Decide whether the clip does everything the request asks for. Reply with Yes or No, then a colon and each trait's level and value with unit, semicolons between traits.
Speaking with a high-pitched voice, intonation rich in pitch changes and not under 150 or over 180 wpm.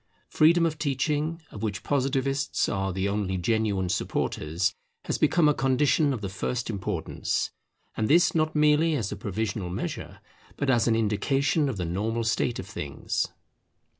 No: low, 115 Hz; wide, 6.7 semitones; average, 160 wpm